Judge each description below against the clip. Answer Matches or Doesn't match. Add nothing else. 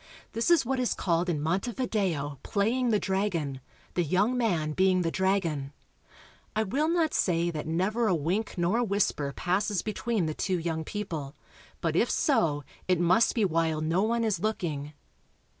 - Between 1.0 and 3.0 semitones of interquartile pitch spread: Doesn't match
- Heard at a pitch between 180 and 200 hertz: Matches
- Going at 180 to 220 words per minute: Doesn't match